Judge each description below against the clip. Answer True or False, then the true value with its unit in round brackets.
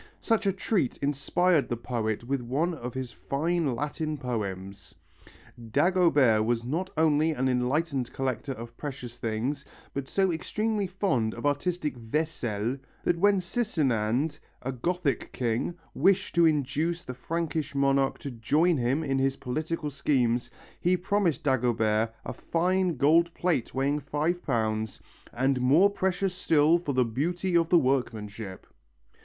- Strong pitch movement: True (5.7 semitones)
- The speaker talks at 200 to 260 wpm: False (140 wpm)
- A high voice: False (140 Hz)